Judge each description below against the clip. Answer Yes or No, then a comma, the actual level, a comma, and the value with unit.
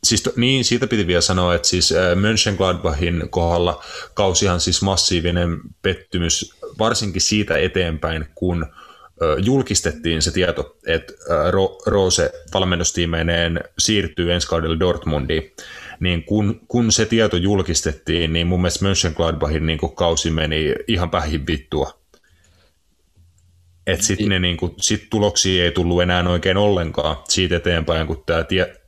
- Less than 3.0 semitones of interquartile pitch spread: Yes, narrow, 2.6 semitones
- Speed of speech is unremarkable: Yes, average, 125 wpm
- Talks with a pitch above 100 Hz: No, very low, 90 Hz